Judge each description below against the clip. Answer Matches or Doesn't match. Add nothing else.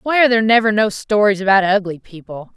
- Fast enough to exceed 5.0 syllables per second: Matches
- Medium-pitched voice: Doesn't match